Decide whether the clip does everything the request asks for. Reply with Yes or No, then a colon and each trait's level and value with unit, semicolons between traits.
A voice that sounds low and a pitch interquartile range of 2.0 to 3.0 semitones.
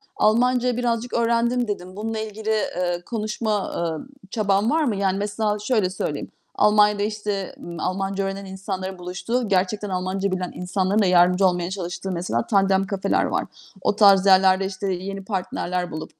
No: high, 195 Hz; narrow, 2.4 semitones